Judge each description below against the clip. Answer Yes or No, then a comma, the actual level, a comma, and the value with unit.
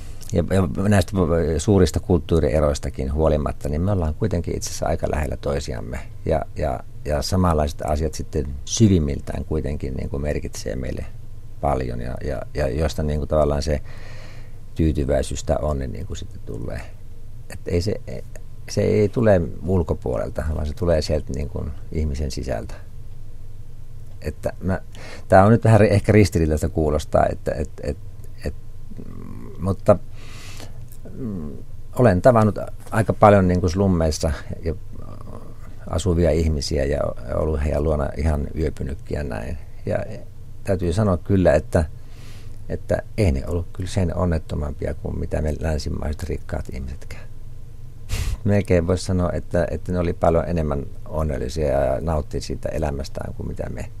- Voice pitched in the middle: No, very low, 90 Hz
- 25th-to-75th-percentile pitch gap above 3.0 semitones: Yes, average, 5.3 semitones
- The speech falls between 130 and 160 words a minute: Yes, average, 135 wpm